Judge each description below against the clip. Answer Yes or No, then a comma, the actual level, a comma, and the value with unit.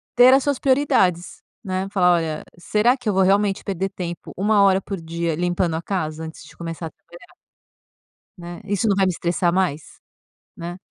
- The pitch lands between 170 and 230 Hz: Yes, medium, 185 Hz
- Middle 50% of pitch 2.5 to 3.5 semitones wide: Yes, average, 2.9 semitones